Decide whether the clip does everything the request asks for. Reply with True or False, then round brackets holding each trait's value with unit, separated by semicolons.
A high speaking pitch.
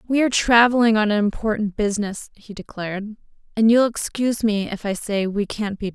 True (215 Hz)